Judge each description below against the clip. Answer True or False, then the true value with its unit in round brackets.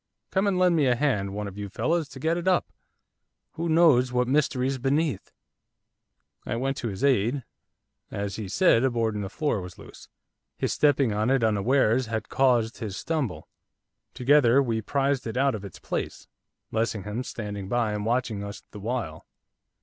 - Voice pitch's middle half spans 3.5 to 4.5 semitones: False (4.9 semitones)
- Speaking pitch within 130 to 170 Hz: False (120 Hz)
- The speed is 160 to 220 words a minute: True (180 wpm)